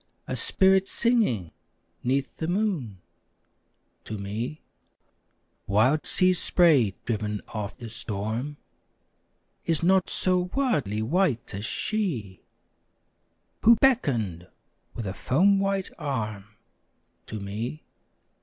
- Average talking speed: No, slow, 100 wpm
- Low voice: Yes, low, 130 Hz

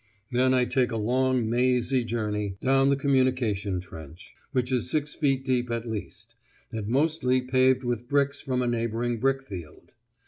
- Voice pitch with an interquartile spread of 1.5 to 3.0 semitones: Yes, narrow, 2.6 semitones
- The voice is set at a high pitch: No, low, 125 Hz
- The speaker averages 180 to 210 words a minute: No, average, 165 wpm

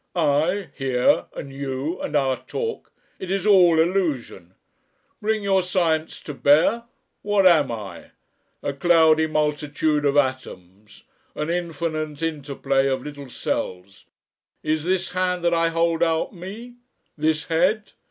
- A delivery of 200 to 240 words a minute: No, slow, 135 wpm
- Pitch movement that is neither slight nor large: Yes, average, 4.2 semitones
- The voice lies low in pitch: No, medium, 160 Hz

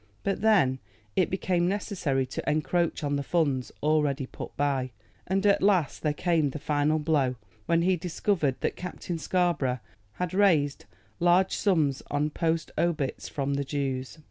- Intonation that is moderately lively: Yes, average, 4.1 semitones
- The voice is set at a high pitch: No, medium, 155 Hz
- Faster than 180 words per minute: No, average, 155 wpm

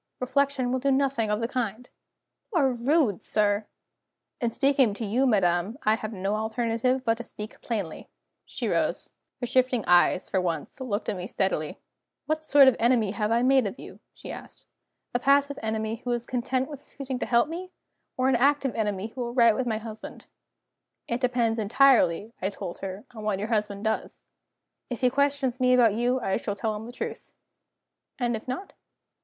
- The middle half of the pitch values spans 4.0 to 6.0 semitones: No, average, 3.5 semitones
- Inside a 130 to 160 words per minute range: No, average, 190 wpm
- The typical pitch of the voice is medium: No, high, 235 Hz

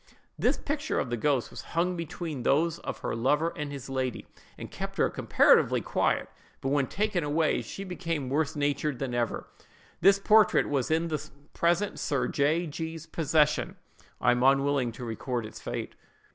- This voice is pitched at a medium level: Yes, medium, 150 Hz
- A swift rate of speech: No, average, 170 wpm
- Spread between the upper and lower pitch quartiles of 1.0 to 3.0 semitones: No, average, 3.9 semitones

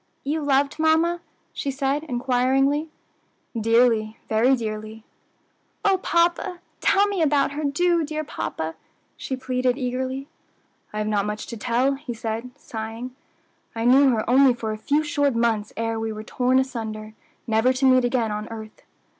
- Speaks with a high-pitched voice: Yes, very high, 255 Hz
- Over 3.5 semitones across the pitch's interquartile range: Yes, average, 4.1 semitones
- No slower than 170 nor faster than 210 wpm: No, average, 155 wpm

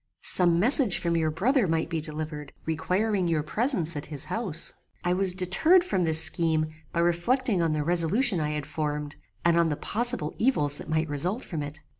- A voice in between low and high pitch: Yes, medium, 170 Hz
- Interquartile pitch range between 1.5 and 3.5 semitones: No, average, 4.0 semitones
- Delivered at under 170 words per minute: No, average, 190 wpm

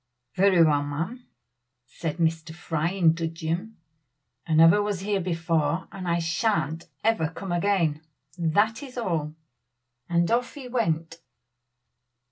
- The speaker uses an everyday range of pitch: Yes, average, 3.8 semitones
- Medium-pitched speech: Yes, medium, 170 Hz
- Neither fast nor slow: No, slow, 130 wpm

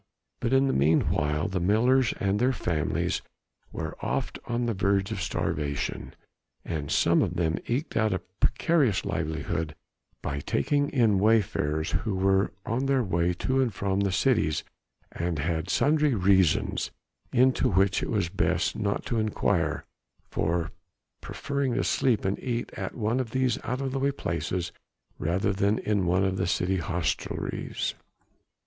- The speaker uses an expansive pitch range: Yes, wide, 5.9 semitones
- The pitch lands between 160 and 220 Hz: No, low, 100 Hz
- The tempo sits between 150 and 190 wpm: Yes, average, 155 wpm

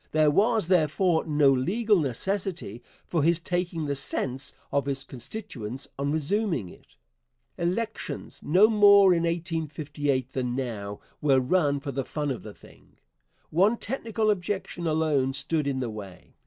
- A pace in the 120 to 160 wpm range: Yes, average, 145 wpm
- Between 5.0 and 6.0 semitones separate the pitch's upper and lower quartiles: Yes, wide, 5.5 semitones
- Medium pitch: Yes, medium, 155 Hz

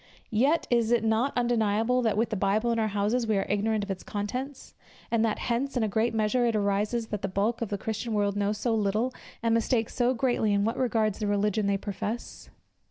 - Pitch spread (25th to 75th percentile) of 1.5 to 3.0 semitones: Yes, narrow, 2.5 semitones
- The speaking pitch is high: Yes, high, 220 Hz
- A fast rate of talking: Yes, fast, 230 wpm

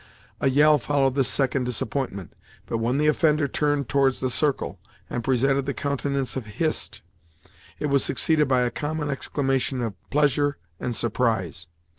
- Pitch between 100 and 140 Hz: Yes, low, 135 Hz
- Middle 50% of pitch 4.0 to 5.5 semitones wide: No, average, 2.7 semitones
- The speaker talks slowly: No, average, 155 wpm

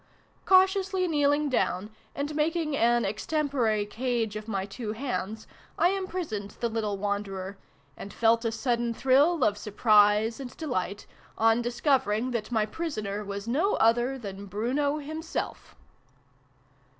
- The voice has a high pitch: Yes, high, 235 Hz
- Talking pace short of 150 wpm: Yes, average, 140 wpm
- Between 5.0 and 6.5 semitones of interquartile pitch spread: Yes, wide, 5.6 semitones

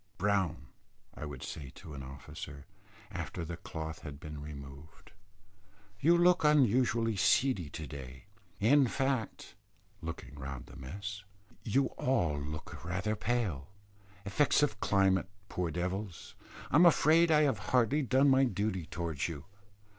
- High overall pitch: No, very low, 95 Hz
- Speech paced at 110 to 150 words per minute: Yes, average, 140 wpm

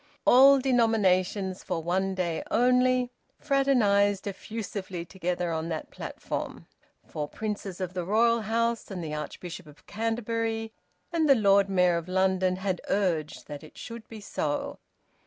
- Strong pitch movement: No, average, 4.1 semitones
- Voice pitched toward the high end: Yes, high, 195 Hz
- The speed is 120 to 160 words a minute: Yes, average, 140 wpm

